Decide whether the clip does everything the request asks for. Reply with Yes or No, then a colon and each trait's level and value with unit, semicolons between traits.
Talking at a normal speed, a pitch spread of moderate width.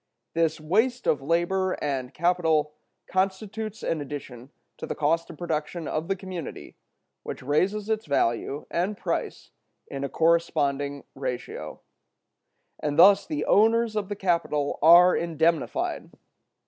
No: slow, 130 wpm; average, 4.7 semitones